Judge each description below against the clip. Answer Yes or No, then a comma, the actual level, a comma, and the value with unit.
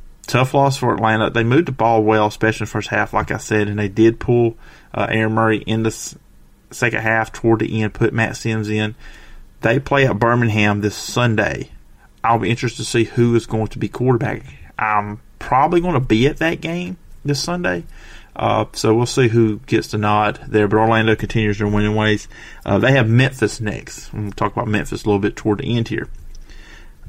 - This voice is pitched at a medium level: No, low, 110 Hz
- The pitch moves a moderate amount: No, narrow, 2.2 semitones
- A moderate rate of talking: No, fast, 210 wpm